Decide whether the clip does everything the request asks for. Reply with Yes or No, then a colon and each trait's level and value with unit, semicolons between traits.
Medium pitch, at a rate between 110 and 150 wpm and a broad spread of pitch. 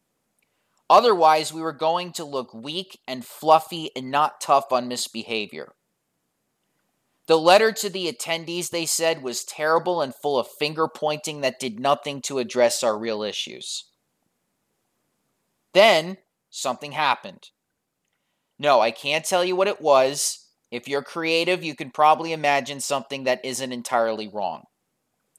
No: medium, 145 Hz; average, 140 wpm; average, 4.1 semitones